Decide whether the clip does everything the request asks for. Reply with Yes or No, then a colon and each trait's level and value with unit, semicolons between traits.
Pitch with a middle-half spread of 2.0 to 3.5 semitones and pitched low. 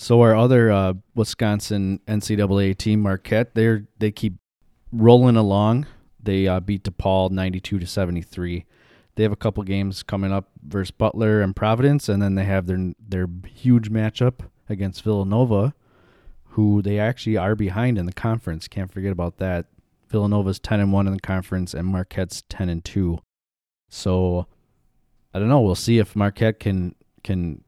Yes: average, 2.8 semitones; low, 100 Hz